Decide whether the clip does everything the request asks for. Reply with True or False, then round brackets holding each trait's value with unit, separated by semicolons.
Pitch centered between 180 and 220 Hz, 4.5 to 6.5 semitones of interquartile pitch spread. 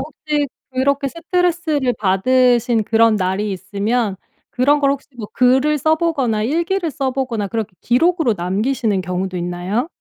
False (250 Hz; 5.8 semitones)